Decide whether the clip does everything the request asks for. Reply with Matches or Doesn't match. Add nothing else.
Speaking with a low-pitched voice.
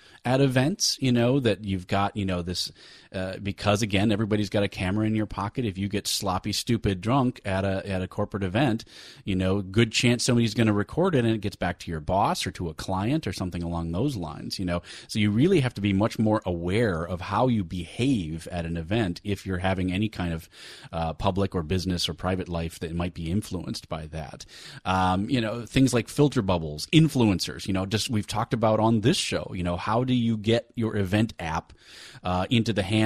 Matches